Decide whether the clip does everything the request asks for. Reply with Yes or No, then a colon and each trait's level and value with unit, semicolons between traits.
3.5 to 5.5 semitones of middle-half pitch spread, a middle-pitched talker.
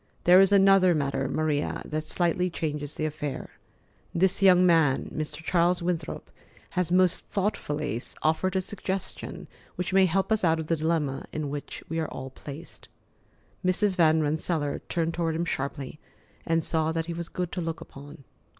No: average, 3.0 semitones; medium, 165 Hz